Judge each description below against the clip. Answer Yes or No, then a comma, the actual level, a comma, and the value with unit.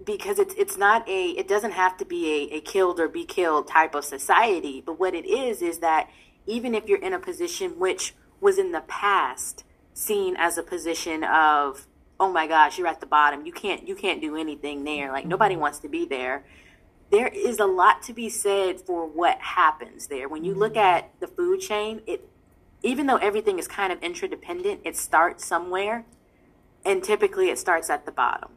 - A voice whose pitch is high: Yes, high, 220 Hz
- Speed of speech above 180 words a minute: Yes, fast, 205 wpm